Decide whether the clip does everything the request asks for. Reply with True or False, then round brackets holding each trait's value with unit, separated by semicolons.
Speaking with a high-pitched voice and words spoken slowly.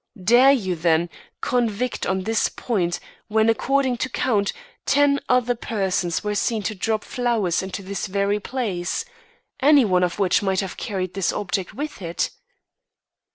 False (210 Hz; 155 wpm)